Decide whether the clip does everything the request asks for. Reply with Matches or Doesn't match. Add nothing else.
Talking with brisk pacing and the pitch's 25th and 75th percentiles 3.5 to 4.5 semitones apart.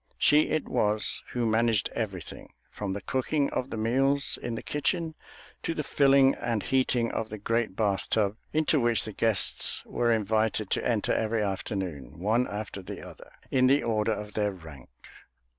Doesn't match